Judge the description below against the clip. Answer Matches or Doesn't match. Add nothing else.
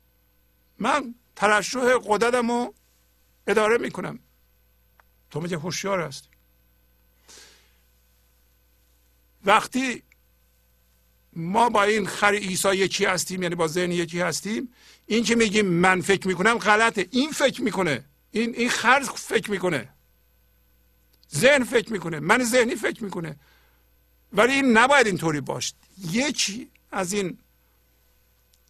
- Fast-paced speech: Doesn't match